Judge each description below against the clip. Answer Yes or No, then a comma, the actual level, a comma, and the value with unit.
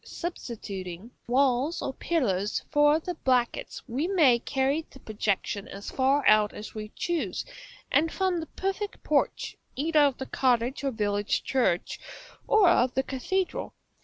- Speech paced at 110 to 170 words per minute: Yes, average, 145 wpm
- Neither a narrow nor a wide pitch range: No, wide, 6.6 semitones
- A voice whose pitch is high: Yes, very high, 265 Hz